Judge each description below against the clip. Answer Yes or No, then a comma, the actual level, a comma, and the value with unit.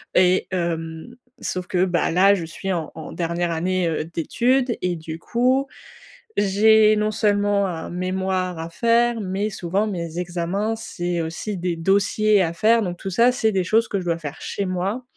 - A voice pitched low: No, medium, 185 Hz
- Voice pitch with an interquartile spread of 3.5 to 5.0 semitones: Yes, average, 3.8 semitones